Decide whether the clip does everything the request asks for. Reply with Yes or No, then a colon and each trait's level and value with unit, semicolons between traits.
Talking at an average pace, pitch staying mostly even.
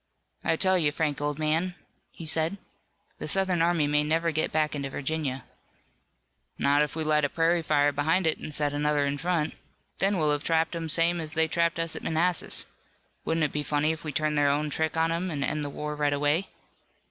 No: fast, 215 wpm; narrow, 2.1 semitones